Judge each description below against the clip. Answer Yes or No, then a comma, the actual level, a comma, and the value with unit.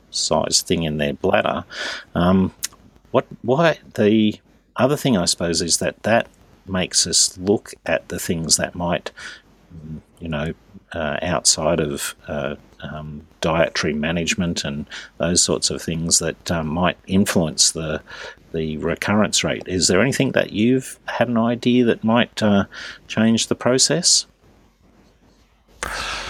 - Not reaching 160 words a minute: Yes, slow, 135 wpm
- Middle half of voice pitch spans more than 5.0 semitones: Yes, wide, 5.6 semitones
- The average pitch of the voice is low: Yes, very low, 95 Hz